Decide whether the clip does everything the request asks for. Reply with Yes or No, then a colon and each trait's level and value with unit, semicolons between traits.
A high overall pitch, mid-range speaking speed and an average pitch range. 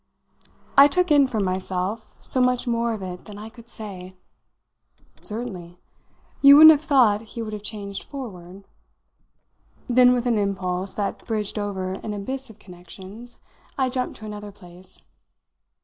Yes: high, 210 Hz; average, 150 wpm; average, 4.5 semitones